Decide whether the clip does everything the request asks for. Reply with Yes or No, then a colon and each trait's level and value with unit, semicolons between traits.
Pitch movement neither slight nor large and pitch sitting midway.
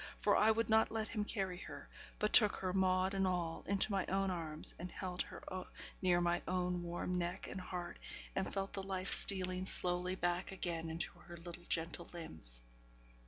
No: narrow, 1.8 semitones; medium, 180 Hz